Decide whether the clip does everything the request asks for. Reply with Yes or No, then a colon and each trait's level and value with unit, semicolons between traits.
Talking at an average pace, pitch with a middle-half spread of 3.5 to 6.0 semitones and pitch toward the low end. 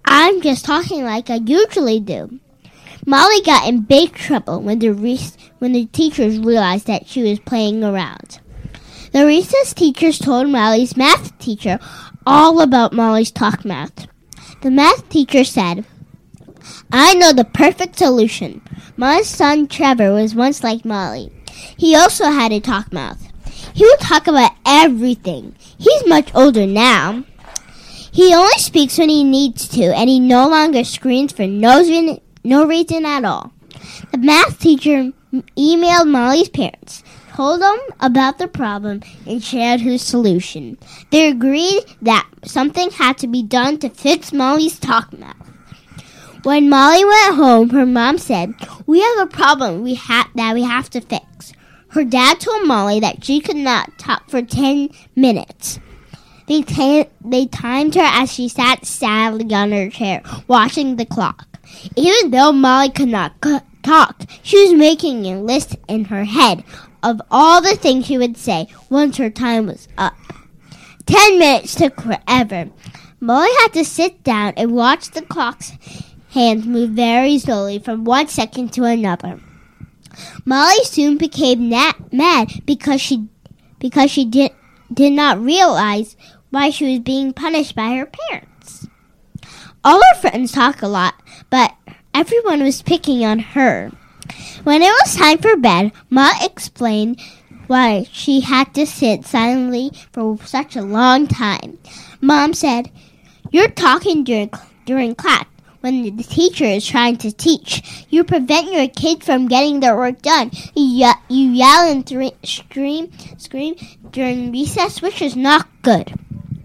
No: average, 150 wpm; average, 4.8 semitones; very high, 260 Hz